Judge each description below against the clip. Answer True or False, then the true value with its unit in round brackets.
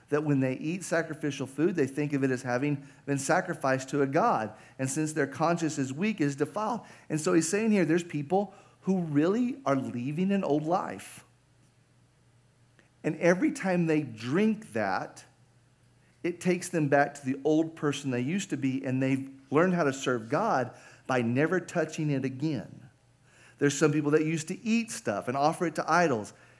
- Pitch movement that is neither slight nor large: True (4.4 semitones)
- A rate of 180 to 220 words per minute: True (185 wpm)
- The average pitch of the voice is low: False (145 Hz)